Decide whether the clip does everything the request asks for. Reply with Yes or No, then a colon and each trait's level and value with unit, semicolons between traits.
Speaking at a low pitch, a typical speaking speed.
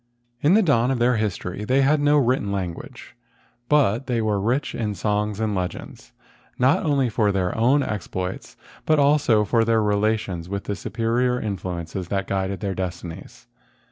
Yes: low, 110 Hz; average, 170 wpm